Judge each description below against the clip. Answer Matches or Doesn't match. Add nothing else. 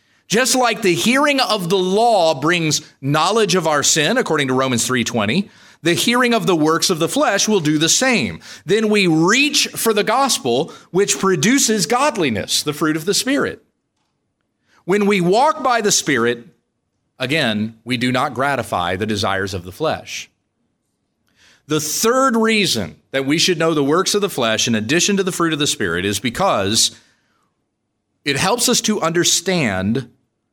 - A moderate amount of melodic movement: Doesn't match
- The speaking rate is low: Doesn't match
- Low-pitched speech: Doesn't match